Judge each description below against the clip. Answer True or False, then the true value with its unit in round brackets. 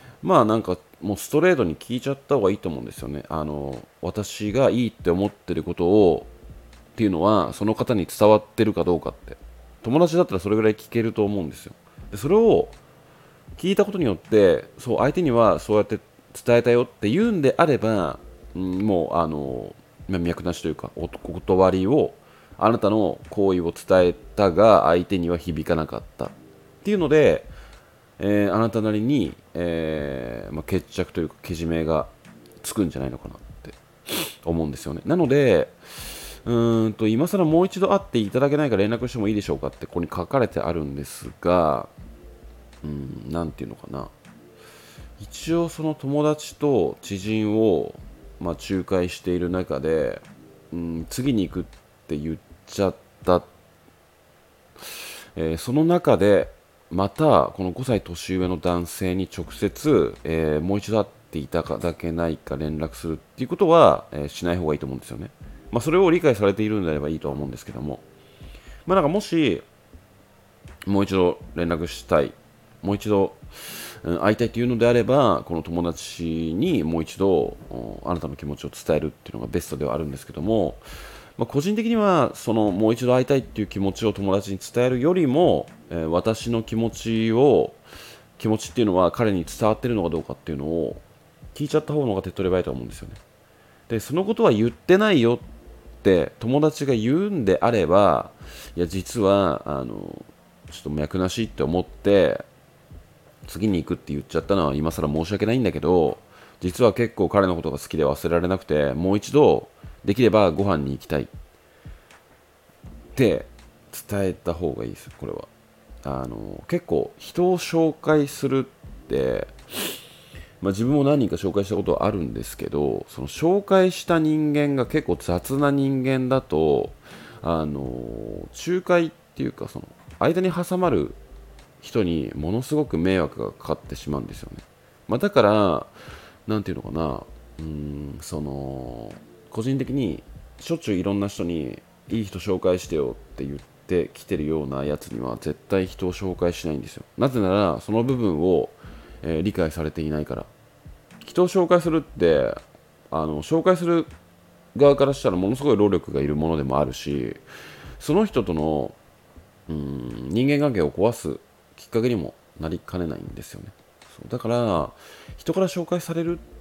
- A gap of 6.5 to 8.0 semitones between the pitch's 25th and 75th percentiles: True (7.0 semitones)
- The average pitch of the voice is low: True (95 Hz)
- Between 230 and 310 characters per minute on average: False (335 characters per minute)